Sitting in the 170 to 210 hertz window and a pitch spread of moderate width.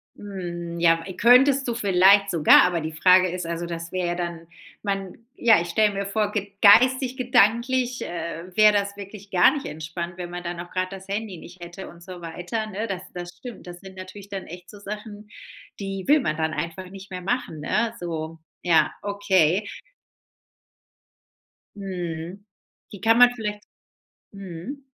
Yes: high, 190 Hz; average, 3.3 semitones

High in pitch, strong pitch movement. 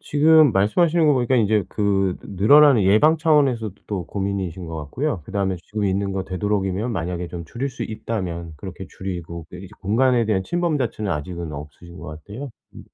No: low, 100 Hz; wide, 5.7 semitones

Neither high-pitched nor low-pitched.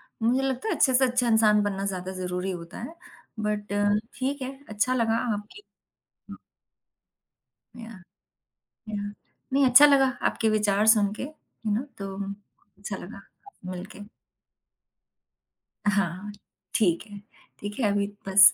No: high, 210 Hz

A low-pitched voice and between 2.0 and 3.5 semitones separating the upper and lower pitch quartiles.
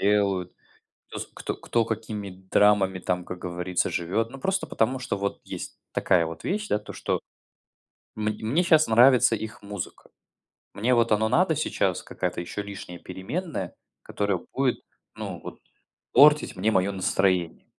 No: low, 105 Hz; average, 4.4 semitones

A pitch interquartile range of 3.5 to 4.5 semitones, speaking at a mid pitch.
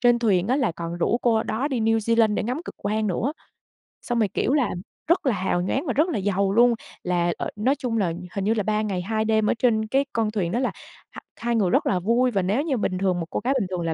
No: average, 4.1 semitones; high, 220 Hz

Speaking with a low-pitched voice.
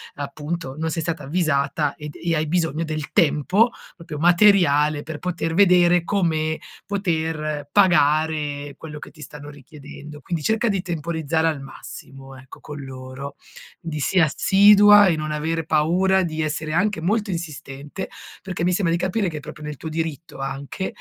No: medium, 160 Hz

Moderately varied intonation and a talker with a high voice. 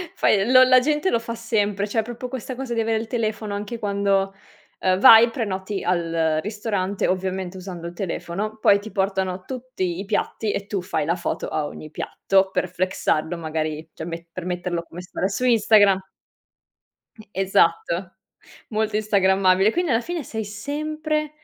Yes: average, 3.6 semitones; high, 200 Hz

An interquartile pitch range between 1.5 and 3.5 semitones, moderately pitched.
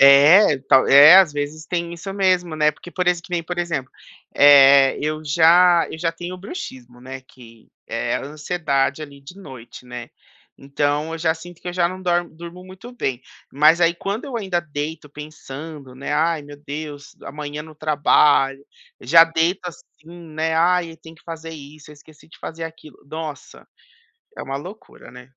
Yes: average, 3.2 semitones; medium, 155 Hz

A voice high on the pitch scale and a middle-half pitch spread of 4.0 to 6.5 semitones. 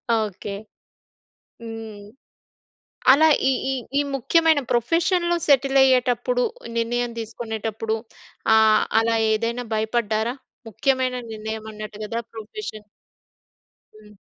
No: high, 230 Hz; average, 3.3 semitones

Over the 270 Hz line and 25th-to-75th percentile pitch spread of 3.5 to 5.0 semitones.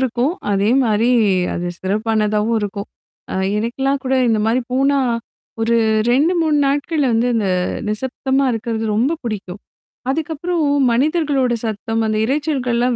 No: high, 240 Hz; average, 4.2 semitones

